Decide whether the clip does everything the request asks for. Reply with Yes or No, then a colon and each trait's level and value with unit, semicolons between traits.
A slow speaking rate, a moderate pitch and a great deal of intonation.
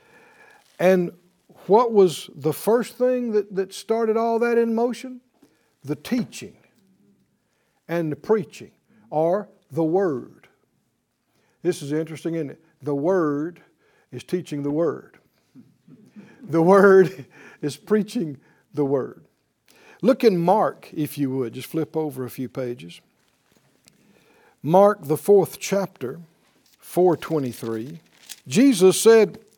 Yes: slow, 115 wpm; medium, 180 Hz; wide, 6.2 semitones